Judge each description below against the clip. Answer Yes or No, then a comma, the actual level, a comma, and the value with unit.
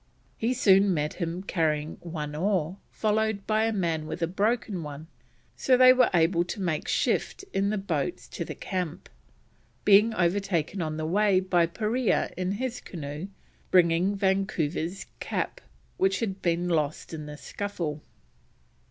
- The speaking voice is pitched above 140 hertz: Yes, medium, 185 Hz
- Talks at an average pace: Yes, average, 150 wpm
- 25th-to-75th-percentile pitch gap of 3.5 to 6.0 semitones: Yes, average, 3.8 semitones